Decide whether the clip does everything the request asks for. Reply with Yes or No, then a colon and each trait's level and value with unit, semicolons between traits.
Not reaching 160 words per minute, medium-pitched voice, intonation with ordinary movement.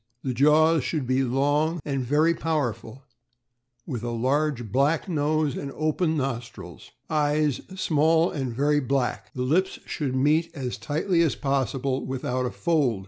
Yes: average, 145 wpm; medium, 145 Hz; average, 3.3 semitones